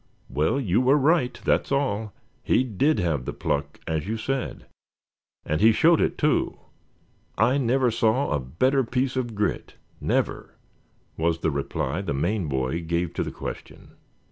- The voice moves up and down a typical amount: No, wide, 8.4 semitones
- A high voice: No, low, 110 Hz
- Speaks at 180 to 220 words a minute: No, average, 160 wpm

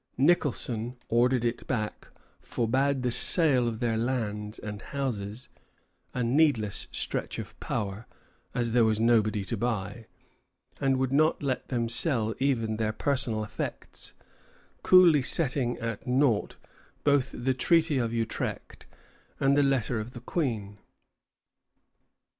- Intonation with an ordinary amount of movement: Yes, average, 3.5 semitones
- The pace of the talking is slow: Yes, slow, 130 wpm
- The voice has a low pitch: Yes, low, 120 Hz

